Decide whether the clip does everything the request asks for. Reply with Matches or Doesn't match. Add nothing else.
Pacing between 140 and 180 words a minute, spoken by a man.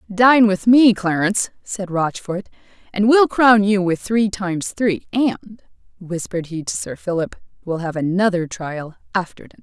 Doesn't match